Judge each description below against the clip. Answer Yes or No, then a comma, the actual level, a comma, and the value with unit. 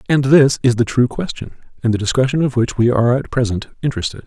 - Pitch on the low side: Yes, low, 125 Hz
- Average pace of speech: No, fast, 225 wpm